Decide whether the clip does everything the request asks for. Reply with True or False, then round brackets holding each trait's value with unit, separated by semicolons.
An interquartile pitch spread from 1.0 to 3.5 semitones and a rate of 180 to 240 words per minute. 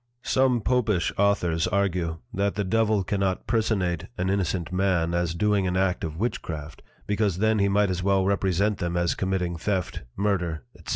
False (2.7 semitones; 170 wpm)